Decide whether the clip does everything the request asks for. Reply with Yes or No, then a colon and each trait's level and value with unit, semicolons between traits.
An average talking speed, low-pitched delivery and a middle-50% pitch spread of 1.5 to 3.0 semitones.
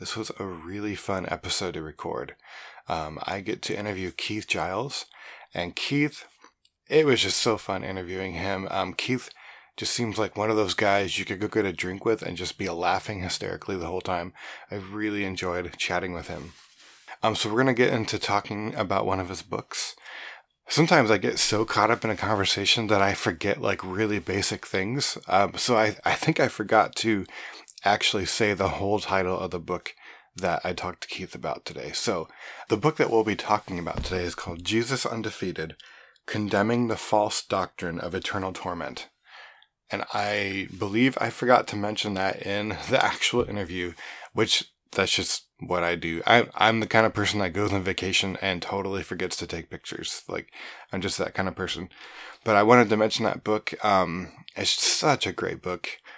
Yes: average, 190 wpm; low, 100 Hz; average, 2.7 semitones